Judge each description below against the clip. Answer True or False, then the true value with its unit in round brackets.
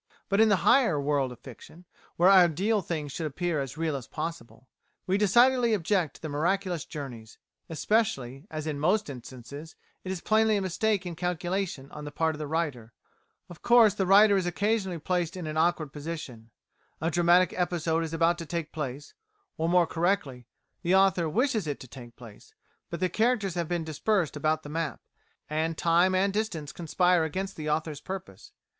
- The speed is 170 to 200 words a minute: True (180 wpm)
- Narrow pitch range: False (4.1 semitones)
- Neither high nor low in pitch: True (170 Hz)